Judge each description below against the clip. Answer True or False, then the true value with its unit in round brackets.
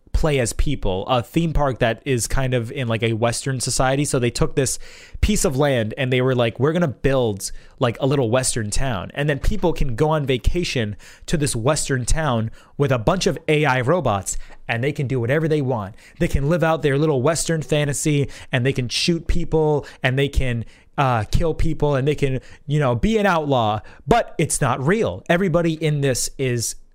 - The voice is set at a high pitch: False (135 Hz)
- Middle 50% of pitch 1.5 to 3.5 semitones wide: False (4.3 semitones)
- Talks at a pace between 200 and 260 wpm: True (205 wpm)